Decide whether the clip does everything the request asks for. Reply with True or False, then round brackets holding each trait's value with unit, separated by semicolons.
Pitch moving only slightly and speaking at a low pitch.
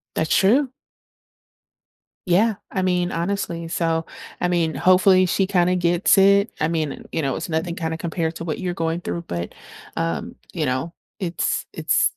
False (2.3 semitones; 175 Hz)